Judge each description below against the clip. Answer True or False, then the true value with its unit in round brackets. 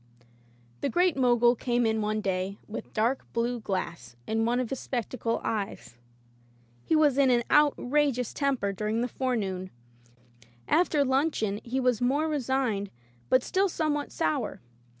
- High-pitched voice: True (245 Hz)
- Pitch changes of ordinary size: True (4.2 semitones)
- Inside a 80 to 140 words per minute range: False (150 wpm)